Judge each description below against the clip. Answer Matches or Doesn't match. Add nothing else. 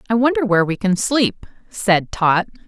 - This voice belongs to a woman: Matches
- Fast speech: Doesn't match